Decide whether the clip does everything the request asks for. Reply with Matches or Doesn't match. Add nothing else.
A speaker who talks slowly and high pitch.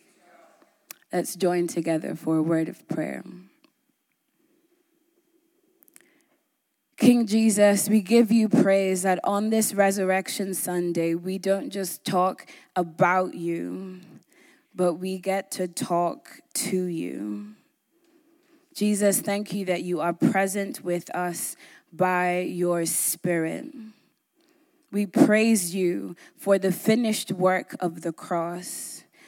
Matches